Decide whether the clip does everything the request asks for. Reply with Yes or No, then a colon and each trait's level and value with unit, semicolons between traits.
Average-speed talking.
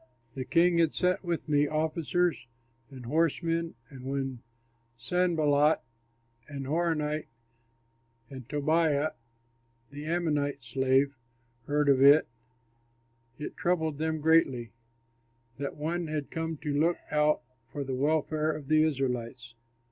No: slow, 115 wpm